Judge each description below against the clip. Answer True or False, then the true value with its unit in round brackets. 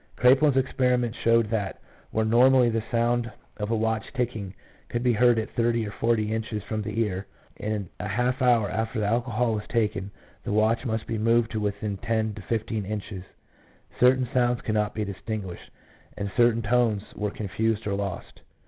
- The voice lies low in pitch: True (110 Hz)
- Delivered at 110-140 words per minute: False (175 wpm)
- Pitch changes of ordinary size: False (2.2 semitones)